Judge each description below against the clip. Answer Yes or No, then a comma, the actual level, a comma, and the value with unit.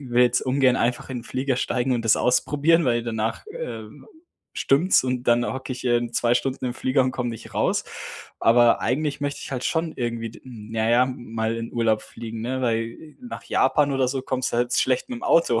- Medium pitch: No, low, 125 Hz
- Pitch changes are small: Yes, narrow, 2.2 semitones